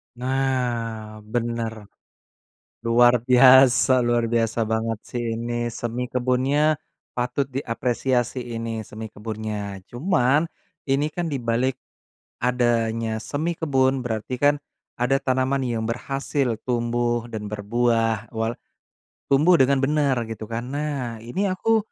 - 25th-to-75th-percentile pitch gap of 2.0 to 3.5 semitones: Yes, average, 2.7 semitones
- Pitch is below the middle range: Yes, low, 120 Hz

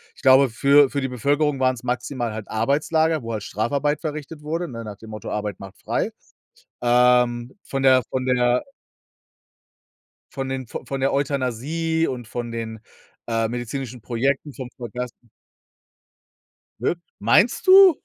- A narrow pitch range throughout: No, average, 3.3 semitones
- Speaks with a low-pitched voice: Yes, low, 130 Hz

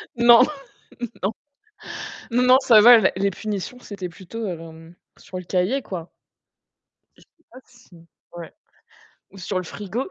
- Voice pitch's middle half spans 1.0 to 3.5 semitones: No, average, 4.8 semitones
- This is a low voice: No, high, 200 Hz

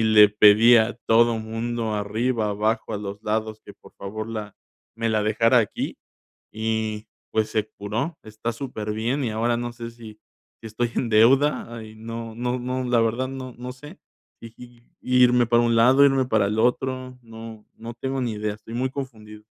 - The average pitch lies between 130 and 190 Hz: No, low, 115 Hz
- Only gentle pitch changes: Yes, narrow, 2.1 semitones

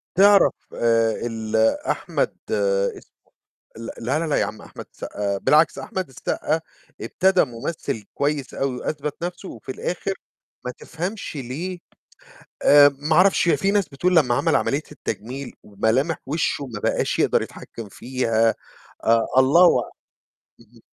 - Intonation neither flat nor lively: No, wide, 6.4 semitones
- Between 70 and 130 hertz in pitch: No, medium, 140 Hz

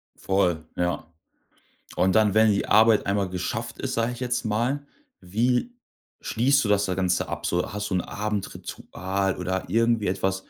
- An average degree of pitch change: Yes, average, 3.5 semitones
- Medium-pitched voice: No, low, 105 Hz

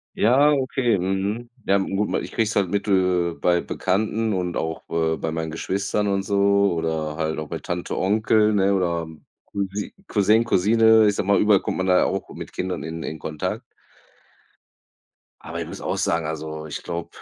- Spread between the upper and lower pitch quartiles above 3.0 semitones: Yes, average, 4.0 semitones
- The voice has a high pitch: No, very low, 95 Hz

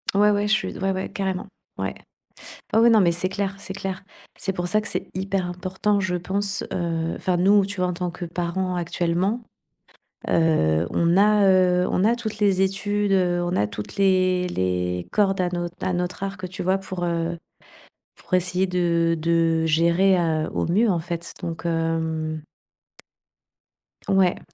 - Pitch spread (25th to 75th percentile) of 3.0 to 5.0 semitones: No, narrow, 2.4 semitones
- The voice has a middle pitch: Yes, medium, 180 Hz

